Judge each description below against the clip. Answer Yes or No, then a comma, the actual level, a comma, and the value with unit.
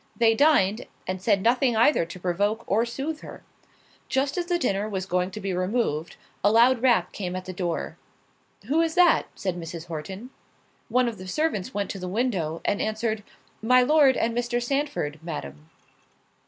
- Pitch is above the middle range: Yes, high, 215 Hz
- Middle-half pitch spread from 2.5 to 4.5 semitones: No, wide, 5.5 semitones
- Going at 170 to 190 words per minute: Yes, average, 175 wpm